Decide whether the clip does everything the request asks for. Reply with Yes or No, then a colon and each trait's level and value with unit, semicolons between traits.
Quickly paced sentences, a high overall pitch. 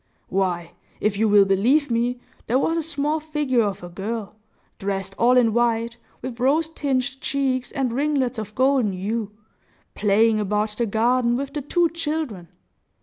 No: average, 160 wpm; high, 235 Hz